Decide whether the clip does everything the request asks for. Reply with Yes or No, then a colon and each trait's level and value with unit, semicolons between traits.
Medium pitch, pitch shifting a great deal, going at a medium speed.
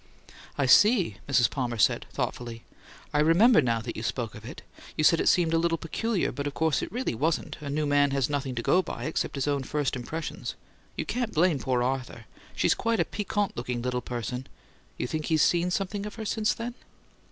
No: medium, 145 Hz; wide, 6.1 semitones; fast, 210 wpm